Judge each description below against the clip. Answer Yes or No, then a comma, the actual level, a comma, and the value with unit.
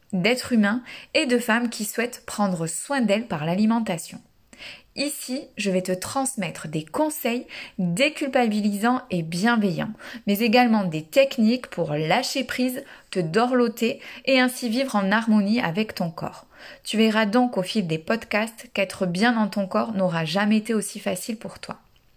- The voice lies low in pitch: No, high, 220 Hz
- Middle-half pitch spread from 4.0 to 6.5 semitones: Yes, average, 4.5 semitones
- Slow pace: No, average, 155 wpm